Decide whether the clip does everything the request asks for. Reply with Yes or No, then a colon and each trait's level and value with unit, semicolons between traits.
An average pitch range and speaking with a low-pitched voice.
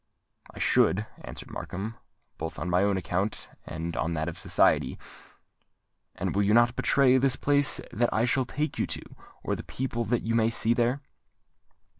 Yes: average, 4.7 semitones; low, 115 Hz